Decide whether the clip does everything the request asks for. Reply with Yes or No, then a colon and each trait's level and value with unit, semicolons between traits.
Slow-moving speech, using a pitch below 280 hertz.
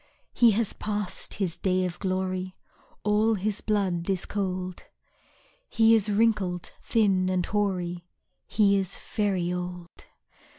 Yes: slow, 125 wpm; high, 190 Hz